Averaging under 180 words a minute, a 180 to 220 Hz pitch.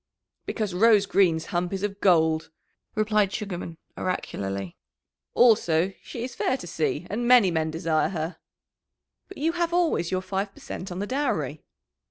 Yes: average, 160 wpm; high, 190 Hz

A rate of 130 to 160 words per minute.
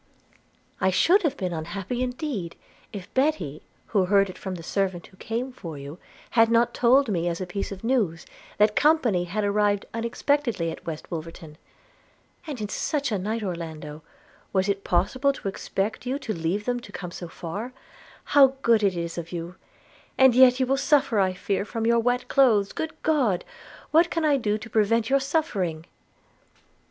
No: average, 185 wpm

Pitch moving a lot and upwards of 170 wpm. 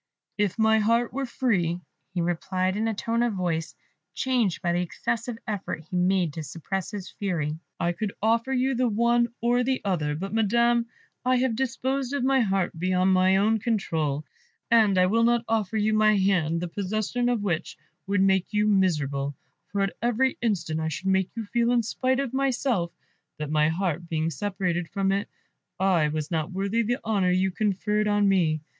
No: average, 4.7 semitones; average, 190 wpm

